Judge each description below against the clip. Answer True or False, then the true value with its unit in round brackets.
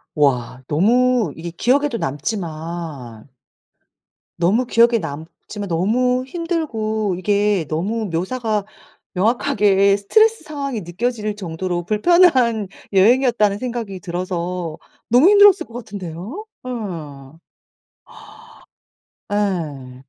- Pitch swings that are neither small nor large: False (6.1 semitones)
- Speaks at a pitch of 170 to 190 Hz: False (205 Hz)